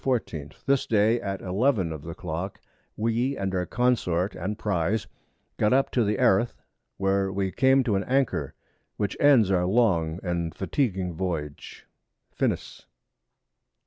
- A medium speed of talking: Yes, average, 145 wpm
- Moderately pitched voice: No, low, 100 Hz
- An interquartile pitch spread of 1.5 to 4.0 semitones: No, average, 5.0 semitones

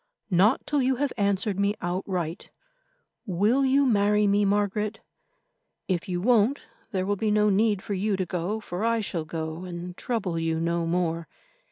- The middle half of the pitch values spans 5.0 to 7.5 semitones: No, average, 3.3 semitones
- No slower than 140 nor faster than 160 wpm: No, average, 170 wpm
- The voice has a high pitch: Yes, high, 200 Hz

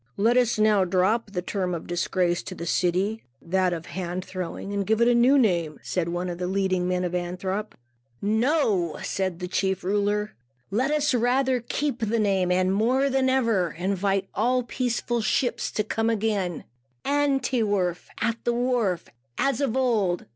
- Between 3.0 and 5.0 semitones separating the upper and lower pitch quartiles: Yes, average, 4.7 semitones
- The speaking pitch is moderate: No, high, 205 Hz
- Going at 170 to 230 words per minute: Yes, average, 180 wpm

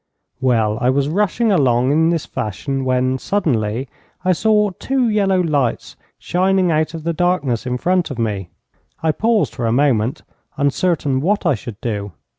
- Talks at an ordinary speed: Yes, average, 165 wpm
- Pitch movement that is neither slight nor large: No, wide, 6.8 semitones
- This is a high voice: No, medium, 145 Hz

